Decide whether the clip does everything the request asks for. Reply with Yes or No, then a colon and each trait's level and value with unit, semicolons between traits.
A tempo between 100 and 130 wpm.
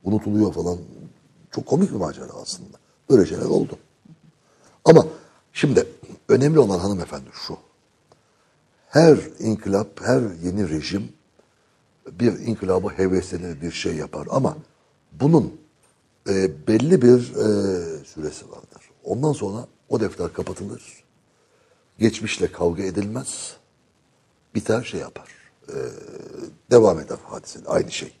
Yes: average, 110 wpm